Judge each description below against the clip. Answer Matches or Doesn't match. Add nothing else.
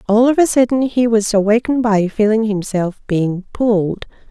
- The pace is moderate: Matches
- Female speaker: Matches